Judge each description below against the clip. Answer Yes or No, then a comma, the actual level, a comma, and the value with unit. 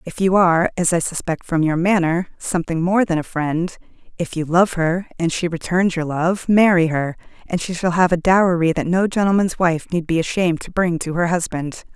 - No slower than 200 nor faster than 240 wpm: Yes, fast, 205 wpm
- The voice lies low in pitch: No, medium, 175 Hz